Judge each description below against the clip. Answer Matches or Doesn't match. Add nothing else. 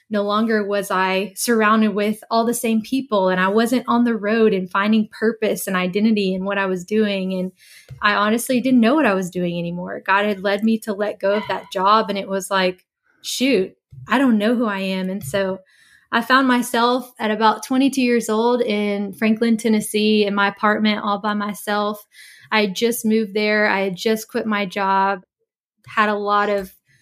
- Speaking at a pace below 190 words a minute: Doesn't match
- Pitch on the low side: Doesn't match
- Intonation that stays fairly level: Matches